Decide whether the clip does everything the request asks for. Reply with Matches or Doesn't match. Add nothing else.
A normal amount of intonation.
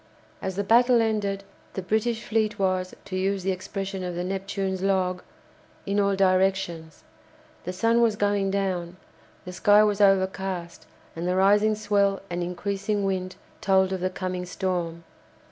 Doesn't match